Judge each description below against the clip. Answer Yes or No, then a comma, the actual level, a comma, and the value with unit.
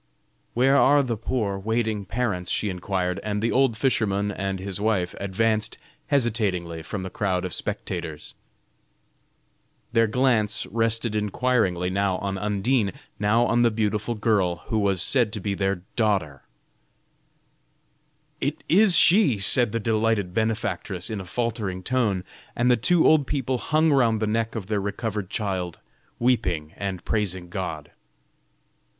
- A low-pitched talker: Yes, low, 105 Hz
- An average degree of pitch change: Yes, average, 3.5 semitones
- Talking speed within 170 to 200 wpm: No, average, 145 wpm